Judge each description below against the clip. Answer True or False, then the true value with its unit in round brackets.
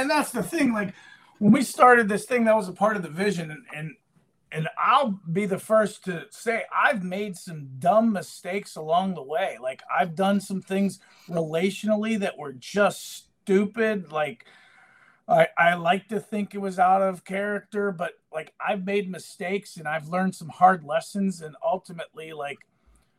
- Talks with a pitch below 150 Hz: False (195 Hz)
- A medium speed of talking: True (180 wpm)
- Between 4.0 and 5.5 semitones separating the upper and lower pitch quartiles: False (3.4 semitones)